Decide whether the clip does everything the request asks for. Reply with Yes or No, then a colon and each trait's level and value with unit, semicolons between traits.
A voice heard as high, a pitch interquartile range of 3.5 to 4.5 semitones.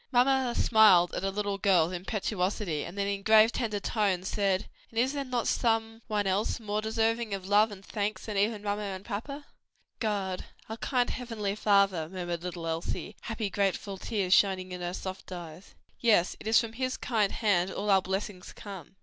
No: high, 205 Hz; average, 2.9 semitones